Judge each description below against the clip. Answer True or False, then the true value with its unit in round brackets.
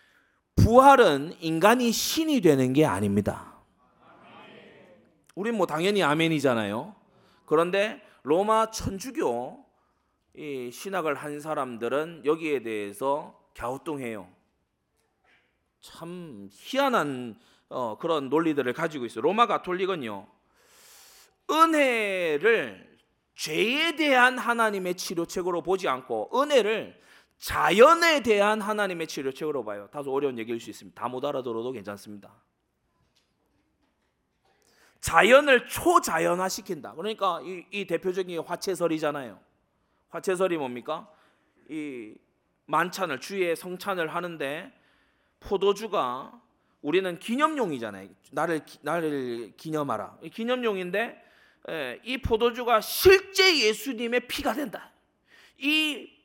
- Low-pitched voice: False (180 Hz)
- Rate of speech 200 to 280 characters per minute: True (245 characters per minute)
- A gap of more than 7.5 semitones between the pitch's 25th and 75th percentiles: True (8.4 semitones)